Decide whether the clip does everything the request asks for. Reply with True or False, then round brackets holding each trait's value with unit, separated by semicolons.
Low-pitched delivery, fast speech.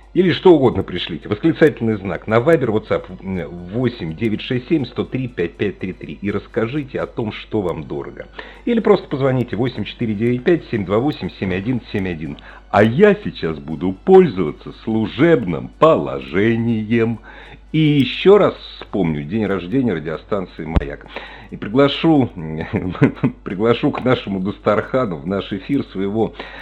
False (115 Hz; 115 wpm)